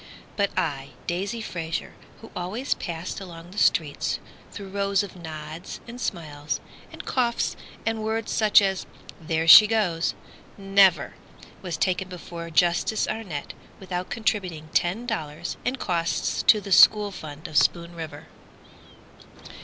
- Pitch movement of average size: Yes, average, 4.0 semitones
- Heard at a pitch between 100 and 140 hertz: No, medium, 180 Hz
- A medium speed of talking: No, slow, 130 wpm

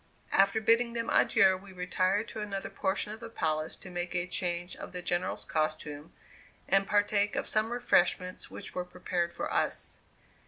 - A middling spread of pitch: Yes, average, 3.0 semitones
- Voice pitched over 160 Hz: Yes, medium, 185 Hz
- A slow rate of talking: No, average, 180 wpm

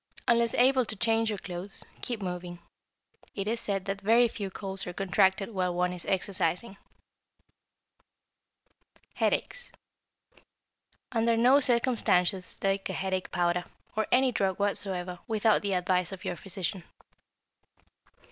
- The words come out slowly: Yes, slow, 130 wpm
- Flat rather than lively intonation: No, average, 3.8 semitones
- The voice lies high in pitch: Yes, high, 195 Hz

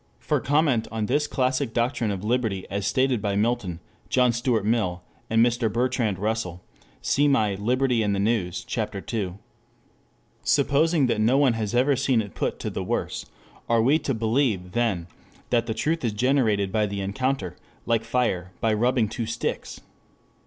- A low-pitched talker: Yes, low, 115 Hz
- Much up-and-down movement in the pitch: No, average, 3.7 semitones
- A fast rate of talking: No, average, 170 wpm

